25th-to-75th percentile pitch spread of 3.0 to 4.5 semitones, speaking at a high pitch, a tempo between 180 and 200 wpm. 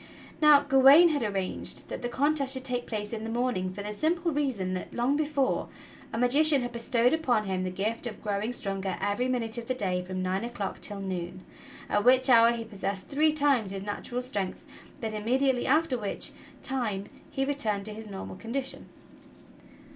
No: average, 4.9 semitones; high, 235 Hz; average, 190 wpm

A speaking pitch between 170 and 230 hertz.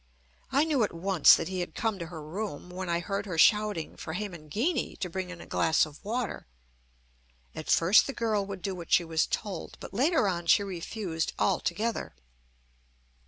Yes: high, 190 Hz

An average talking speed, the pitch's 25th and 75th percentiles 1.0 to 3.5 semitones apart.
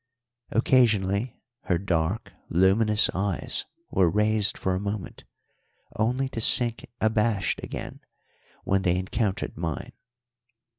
No: slow, 105 wpm; average, 2.9 semitones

